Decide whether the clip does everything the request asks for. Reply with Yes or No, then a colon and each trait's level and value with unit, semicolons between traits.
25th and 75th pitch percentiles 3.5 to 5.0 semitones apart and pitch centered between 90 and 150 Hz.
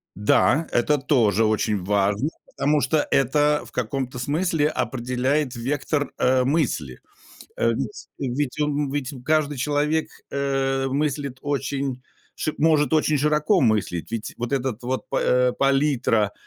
No: average, 3.1 semitones; low, 135 Hz